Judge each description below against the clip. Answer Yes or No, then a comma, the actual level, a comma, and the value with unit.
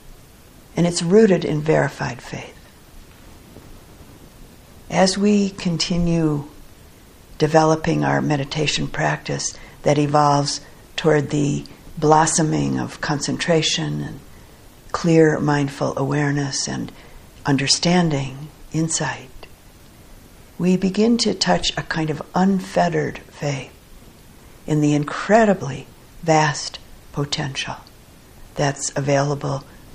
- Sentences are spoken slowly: Yes, slow, 85 wpm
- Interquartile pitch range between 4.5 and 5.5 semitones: No, average, 2.7 semitones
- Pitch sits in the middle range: Yes, medium, 150 Hz